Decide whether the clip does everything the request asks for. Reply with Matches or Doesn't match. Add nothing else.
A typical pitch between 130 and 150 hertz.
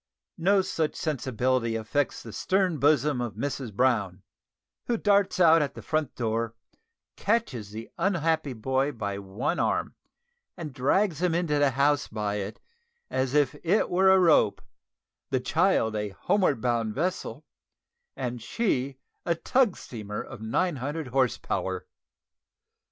Matches